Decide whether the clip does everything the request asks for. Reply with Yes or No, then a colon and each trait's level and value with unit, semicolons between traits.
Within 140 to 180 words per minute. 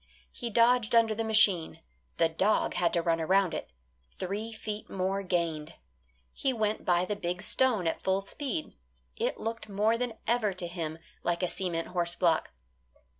Yes: average, 170 wpm